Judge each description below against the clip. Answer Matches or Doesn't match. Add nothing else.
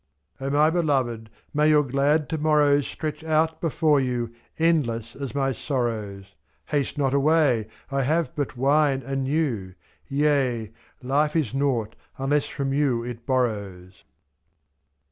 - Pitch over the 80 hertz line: Matches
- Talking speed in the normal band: Matches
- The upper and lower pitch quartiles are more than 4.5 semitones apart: Doesn't match